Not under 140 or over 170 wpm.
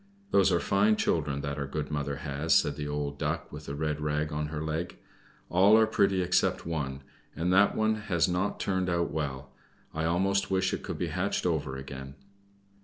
No: average, 190 wpm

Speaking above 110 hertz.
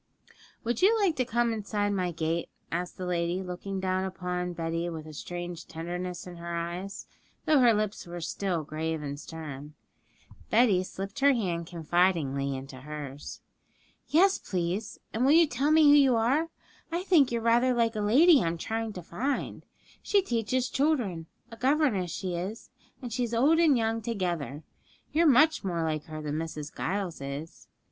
Yes: high, 190 Hz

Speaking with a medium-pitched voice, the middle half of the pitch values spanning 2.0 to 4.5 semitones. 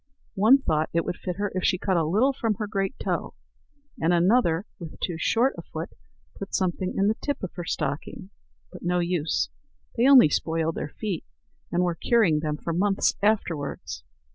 Yes: medium, 180 Hz; average, 4.1 semitones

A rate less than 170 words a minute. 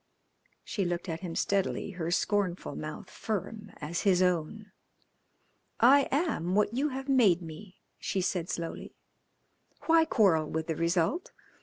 Yes: average, 140 wpm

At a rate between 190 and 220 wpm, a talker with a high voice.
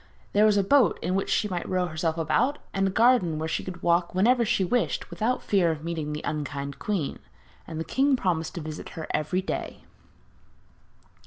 No: average, 195 wpm; medium, 180 Hz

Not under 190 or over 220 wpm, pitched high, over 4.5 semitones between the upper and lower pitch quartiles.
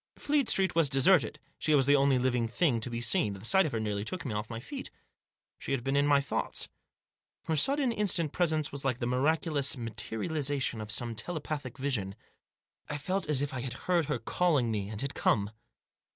No: fast, 205 wpm; medium, 140 Hz; average, 5.1 semitones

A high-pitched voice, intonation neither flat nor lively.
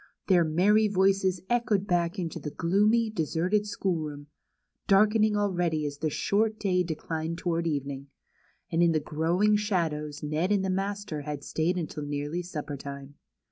No: medium, 175 Hz; average, 4.6 semitones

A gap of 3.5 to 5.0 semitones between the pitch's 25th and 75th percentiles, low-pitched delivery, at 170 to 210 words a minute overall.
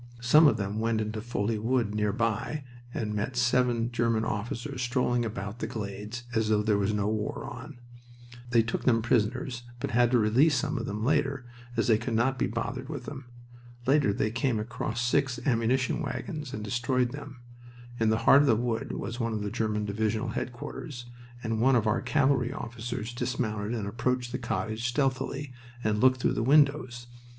No: average, 2.8 semitones; low, 120 Hz; average, 185 wpm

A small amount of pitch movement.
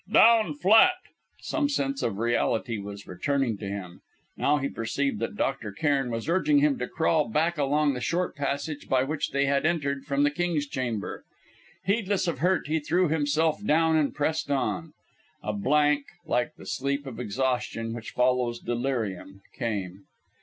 No: average, 5.2 semitones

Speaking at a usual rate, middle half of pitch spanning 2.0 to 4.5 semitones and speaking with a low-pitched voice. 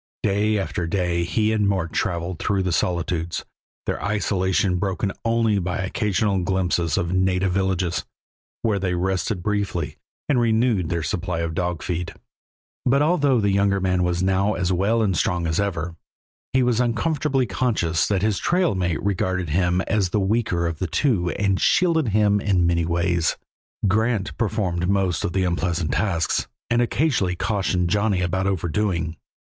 Yes: average, 160 wpm; average, 3.2 semitones; very low, 95 Hz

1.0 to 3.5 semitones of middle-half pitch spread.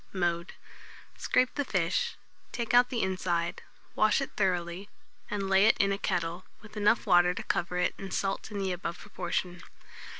Yes: average, 2.9 semitones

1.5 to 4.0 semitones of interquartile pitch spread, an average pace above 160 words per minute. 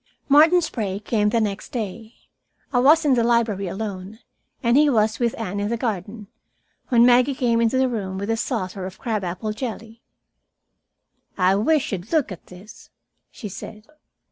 Yes: average, 3.4 semitones; average, 170 wpm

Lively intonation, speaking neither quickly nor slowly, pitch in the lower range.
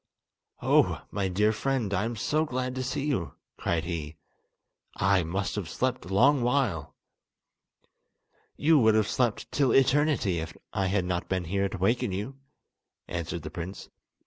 Yes: wide, 6.1 semitones; average, 160 wpm; low, 100 Hz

